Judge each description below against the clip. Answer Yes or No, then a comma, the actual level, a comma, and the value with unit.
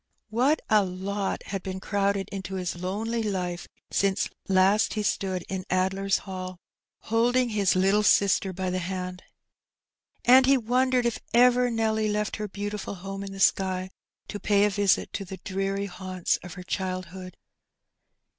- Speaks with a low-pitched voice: No, high, 195 Hz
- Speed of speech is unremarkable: Yes, average, 155 wpm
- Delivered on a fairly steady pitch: Yes, narrow, 2.3 semitones